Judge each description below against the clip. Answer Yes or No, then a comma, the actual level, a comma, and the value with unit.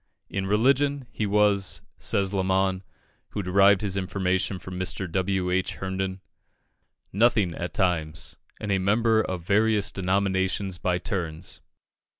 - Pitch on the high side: No, very low, 95 Hz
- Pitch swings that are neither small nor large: No, narrow, 1.6 semitones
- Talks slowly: Yes, slow, 130 wpm